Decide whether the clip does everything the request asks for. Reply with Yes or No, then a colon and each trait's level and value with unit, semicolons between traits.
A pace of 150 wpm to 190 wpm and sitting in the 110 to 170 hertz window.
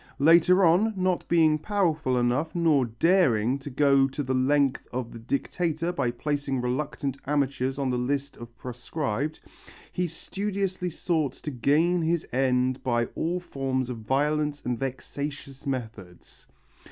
No: average, 140 wpm; medium, 140 Hz